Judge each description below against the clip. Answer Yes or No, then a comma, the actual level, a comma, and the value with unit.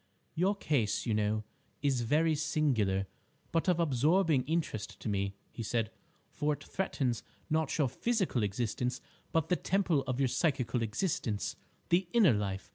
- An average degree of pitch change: No, wide, 6.7 semitones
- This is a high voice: No, low, 135 Hz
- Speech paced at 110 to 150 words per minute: Yes, average, 145 wpm